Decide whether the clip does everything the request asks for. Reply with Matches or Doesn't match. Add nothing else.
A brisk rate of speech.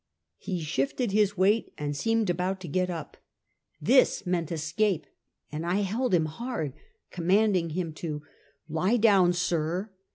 Doesn't match